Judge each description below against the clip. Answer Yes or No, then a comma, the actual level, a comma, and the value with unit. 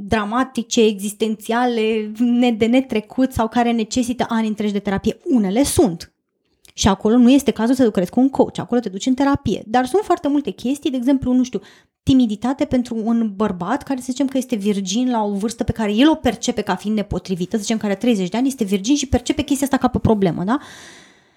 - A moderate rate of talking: No, fast, 210 wpm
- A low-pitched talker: No, high, 235 Hz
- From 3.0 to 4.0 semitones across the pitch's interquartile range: Yes, average, 3.3 semitones